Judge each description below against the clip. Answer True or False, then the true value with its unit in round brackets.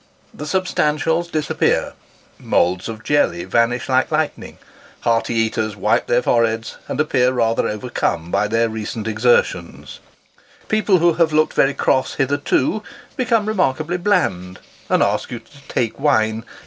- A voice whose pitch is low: True (125 Hz)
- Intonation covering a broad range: True (5.8 semitones)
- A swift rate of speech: False (155 wpm)